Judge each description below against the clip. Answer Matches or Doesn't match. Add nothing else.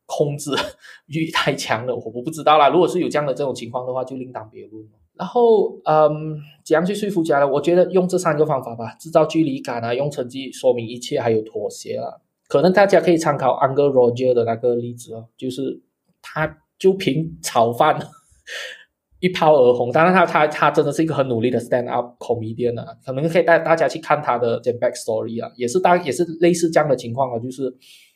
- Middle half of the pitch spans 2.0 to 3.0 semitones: Doesn't match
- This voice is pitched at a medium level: Matches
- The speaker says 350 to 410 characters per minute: Matches